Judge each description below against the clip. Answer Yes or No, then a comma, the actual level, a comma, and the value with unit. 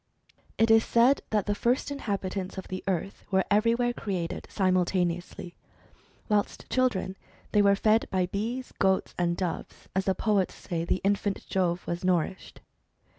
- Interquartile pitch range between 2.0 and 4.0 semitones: Yes, average, 2.9 semitones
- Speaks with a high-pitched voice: Yes, high, 195 Hz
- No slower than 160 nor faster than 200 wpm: No, average, 150 wpm